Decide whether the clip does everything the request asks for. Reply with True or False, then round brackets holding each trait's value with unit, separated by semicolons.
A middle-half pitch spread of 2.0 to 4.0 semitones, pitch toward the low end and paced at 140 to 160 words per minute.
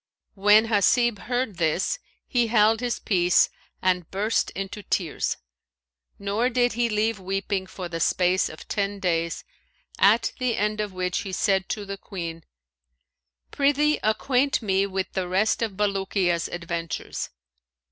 False (3.3 semitones; 200 Hz; 145 wpm)